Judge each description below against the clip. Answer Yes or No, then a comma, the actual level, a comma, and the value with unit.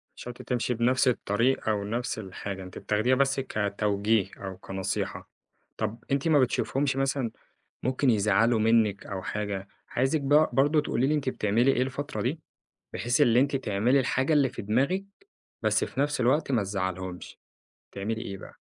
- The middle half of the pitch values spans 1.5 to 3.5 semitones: No, average, 4.7 semitones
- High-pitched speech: No, low, 120 Hz